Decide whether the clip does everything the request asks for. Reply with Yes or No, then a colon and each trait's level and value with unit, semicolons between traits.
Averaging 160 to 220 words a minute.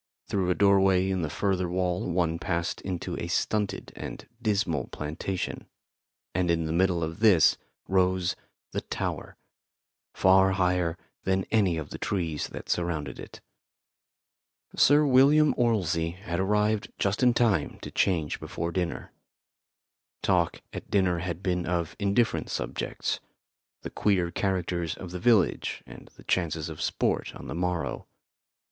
No: average, 140 wpm